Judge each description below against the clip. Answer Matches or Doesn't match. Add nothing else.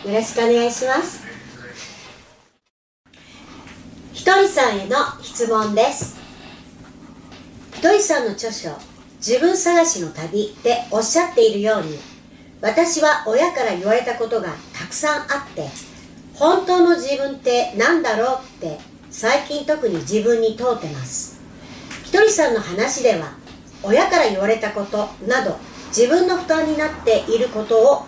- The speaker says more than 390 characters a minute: Doesn't match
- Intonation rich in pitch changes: Matches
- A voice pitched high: Matches